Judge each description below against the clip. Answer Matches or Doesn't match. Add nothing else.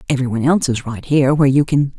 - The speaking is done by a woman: Matches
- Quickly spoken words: Matches